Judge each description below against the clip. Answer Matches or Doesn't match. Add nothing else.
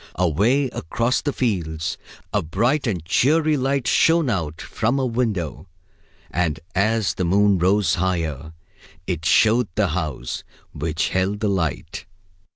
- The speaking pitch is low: Matches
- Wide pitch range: Matches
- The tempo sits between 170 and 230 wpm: Doesn't match